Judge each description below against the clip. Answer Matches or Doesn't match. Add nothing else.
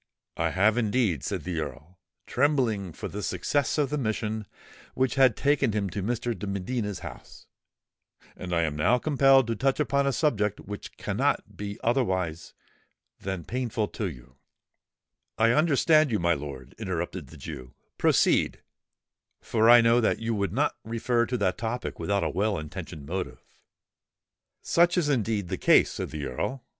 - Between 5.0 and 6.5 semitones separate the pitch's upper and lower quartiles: Matches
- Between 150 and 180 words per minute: Matches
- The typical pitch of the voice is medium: Doesn't match